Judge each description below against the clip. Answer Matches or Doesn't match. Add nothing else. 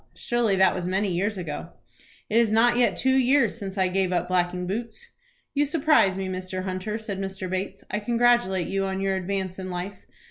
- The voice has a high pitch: Matches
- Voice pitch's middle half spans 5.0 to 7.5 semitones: Doesn't match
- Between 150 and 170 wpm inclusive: Doesn't match